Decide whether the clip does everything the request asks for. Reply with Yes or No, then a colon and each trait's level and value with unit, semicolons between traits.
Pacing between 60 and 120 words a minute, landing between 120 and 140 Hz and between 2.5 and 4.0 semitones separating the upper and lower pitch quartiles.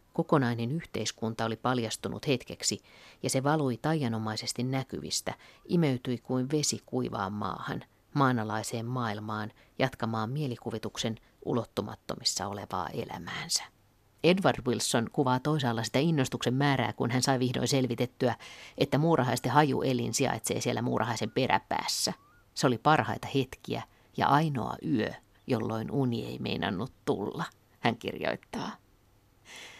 Yes: average, 115 wpm; low, 125 Hz; average, 3.4 semitones